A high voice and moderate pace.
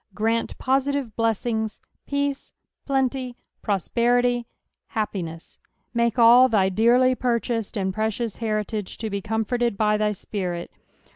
No: high, 230 Hz; slow, 110 wpm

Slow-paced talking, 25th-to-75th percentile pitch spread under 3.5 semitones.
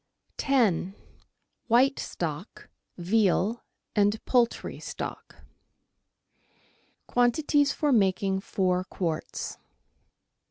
No: slow, 70 wpm; average, 4.5 semitones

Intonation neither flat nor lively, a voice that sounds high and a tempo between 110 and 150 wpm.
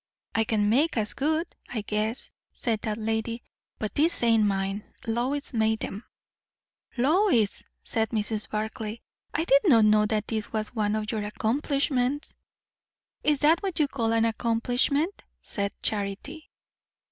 Yes: average, 4.4 semitones; high, 225 Hz; average, 145 wpm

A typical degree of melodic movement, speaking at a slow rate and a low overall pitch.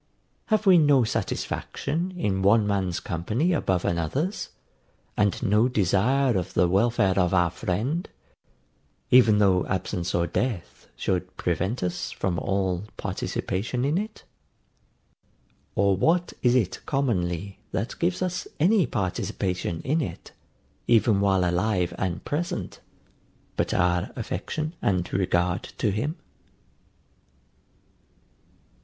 No: wide, 6.4 semitones; slow, 115 wpm; low, 100 Hz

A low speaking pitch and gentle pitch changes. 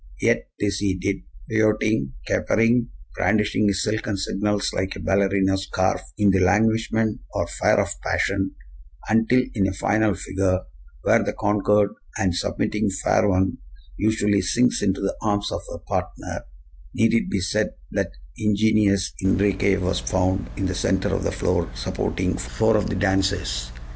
Yes: low, 100 Hz; narrow, 2.0 semitones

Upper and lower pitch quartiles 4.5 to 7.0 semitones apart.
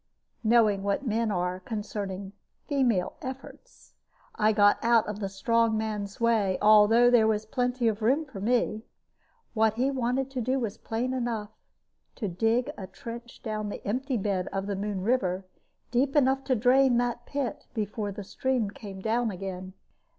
No: average, 3.3 semitones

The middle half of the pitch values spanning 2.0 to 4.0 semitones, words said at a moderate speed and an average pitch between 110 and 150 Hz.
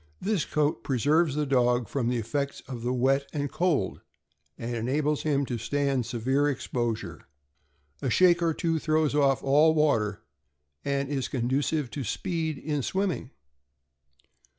Yes: average, 3.6 semitones; average, 150 wpm; medium, 140 Hz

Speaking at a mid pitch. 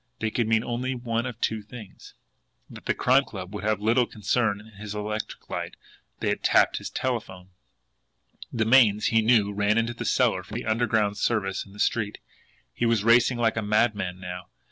No: low, 110 Hz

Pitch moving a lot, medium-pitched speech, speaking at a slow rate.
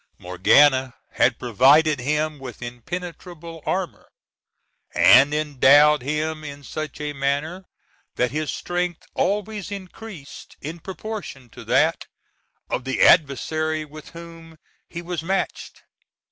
No: average, 3.7 semitones; medium, 155 Hz; slow, 115 wpm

